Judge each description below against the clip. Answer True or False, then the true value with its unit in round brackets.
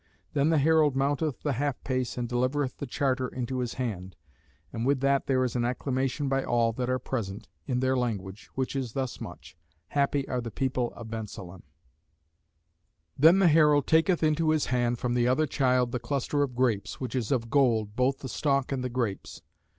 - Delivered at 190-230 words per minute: True (195 wpm)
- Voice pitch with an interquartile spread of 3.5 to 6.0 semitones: False (2.7 semitones)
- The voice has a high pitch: False (130 Hz)